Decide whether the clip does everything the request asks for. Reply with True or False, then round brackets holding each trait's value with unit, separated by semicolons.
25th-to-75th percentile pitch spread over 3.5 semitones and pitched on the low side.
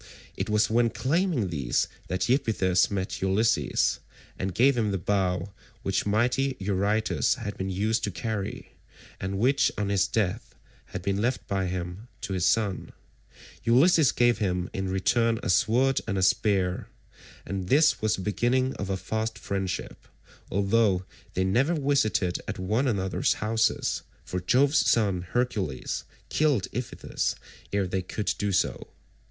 True (4.1 semitones; 105 Hz)